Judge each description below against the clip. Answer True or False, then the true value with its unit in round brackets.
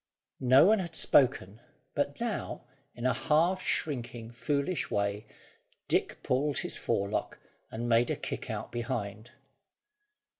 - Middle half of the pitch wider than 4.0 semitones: True (4.5 semitones)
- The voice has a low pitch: True (125 Hz)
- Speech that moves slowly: True (125 wpm)